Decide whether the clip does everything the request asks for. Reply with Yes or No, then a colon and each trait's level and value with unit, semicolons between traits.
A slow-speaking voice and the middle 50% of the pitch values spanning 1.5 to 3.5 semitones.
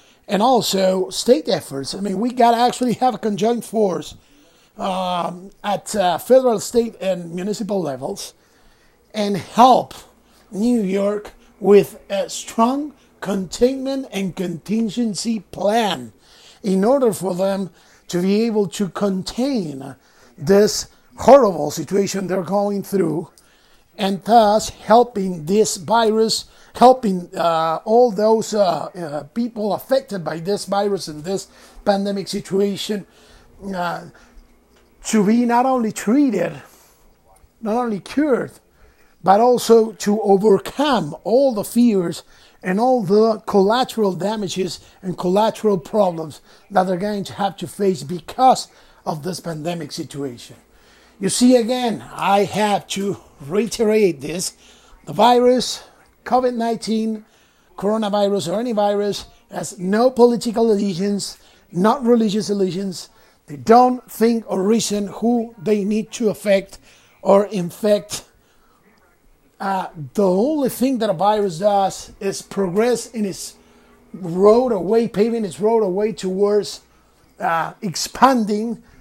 Yes: slow, 120 wpm; average, 3.2 semitones